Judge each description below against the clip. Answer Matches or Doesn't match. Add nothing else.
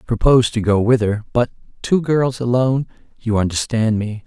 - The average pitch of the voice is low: Matches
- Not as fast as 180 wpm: Matches